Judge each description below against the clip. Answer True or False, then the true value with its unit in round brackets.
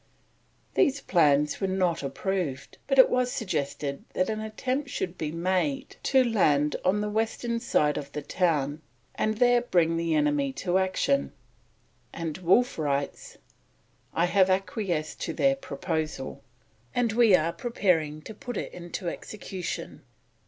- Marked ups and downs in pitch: True (6.2 semitones)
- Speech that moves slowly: False (145 wpm)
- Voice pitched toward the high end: False (180 Hz)